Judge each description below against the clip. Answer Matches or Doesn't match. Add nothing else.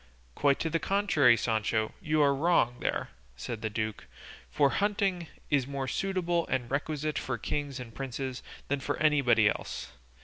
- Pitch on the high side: Doesn't match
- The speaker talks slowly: Doesn't match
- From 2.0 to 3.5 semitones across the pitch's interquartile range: Doesn't match